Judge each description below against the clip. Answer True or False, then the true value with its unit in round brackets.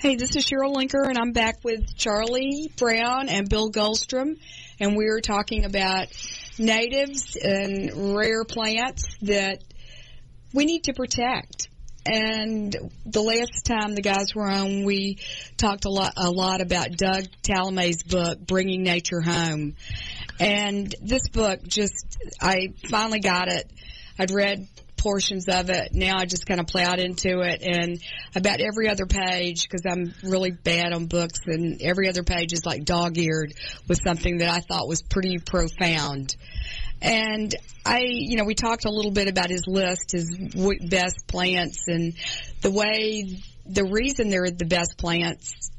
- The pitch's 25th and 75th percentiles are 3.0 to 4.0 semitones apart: True (3.5 semitones)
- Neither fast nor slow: True (160 wpm)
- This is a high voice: True (195 Hz)